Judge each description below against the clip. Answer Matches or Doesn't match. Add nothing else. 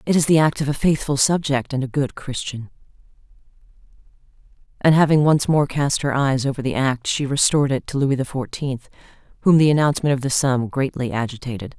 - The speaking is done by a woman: Matches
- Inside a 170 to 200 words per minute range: Matches